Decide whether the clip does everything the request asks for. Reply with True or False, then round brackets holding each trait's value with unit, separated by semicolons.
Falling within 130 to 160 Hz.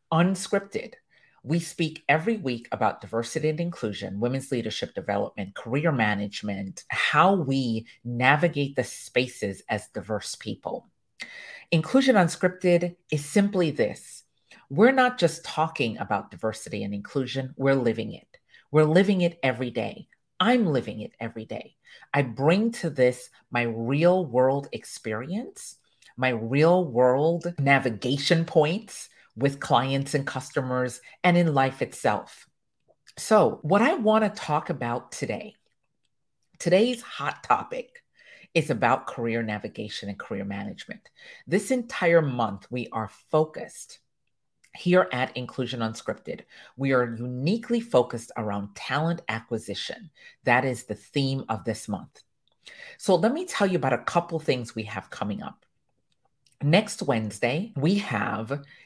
True (135 Hz)